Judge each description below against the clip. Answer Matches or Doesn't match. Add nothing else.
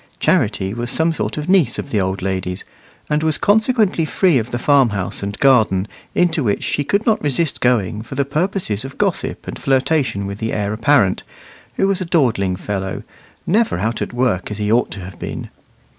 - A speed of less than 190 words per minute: Doesn't match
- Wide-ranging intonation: Matches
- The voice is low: Matches